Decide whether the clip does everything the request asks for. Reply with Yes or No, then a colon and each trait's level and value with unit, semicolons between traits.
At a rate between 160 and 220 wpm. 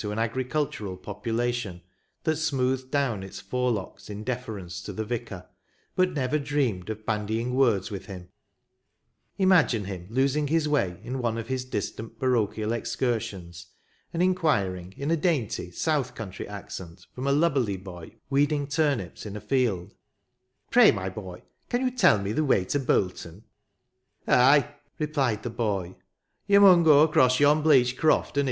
Yes: average, 170 wpm